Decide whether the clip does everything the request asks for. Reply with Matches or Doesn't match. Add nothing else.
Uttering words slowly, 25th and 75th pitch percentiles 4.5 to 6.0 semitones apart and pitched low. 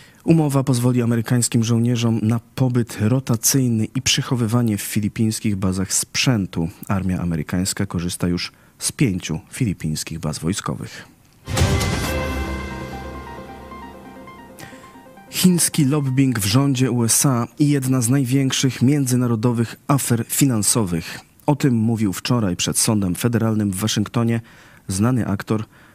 Matches